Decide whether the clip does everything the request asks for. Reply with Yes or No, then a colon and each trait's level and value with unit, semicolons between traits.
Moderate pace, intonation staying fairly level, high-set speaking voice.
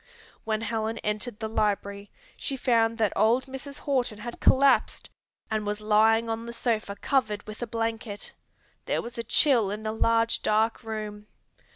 Yes: average, 165 wpm; narrow, 1.7 semitones; high, 225 Hz